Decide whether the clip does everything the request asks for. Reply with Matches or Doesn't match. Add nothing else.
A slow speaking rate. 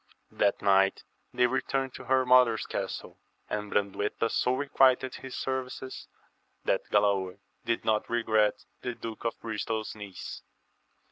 Matches